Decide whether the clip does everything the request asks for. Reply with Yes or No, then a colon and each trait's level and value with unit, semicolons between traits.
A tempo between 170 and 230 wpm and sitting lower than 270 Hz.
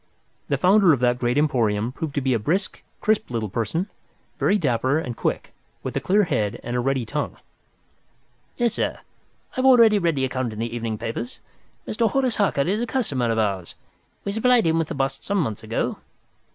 Yes: average, 200 wpm; low, 135 Hz